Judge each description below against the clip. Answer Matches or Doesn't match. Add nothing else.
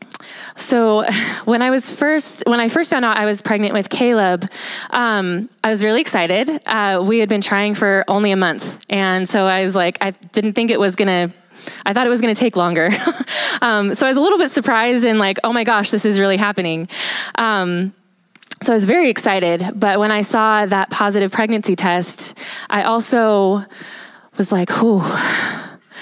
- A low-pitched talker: Doesn't match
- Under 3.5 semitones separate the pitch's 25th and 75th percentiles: Matches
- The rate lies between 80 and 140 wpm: Doesn't match